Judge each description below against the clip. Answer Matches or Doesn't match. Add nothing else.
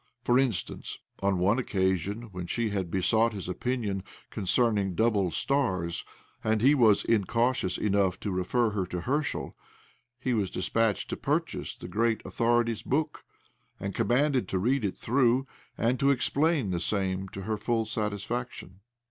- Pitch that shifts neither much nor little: Matches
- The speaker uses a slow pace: Doesn't match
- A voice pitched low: Matches